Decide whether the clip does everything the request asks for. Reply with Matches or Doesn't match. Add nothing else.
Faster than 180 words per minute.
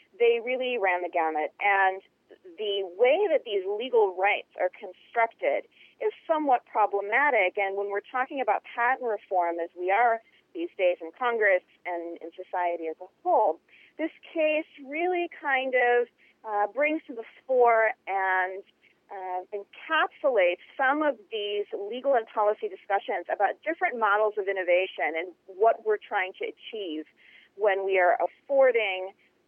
Doesn't match